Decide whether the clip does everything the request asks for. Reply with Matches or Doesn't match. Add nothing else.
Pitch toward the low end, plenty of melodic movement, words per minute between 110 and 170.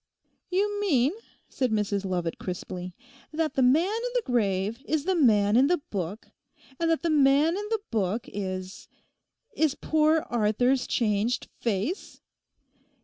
Doesn't match